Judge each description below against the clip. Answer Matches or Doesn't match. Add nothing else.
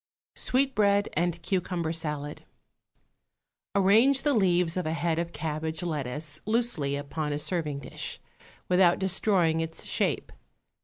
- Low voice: Doesn't match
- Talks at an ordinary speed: Doesn't match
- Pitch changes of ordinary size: Matches